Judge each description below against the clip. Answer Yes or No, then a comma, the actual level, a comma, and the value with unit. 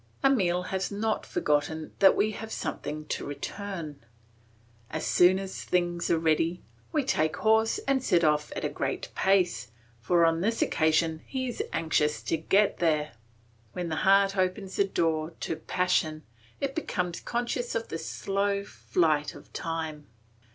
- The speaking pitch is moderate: Yes, medium, 175 Hz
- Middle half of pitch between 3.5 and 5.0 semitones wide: Yes, average, 4.0 semitones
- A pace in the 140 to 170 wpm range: Yes, average, 160 wpm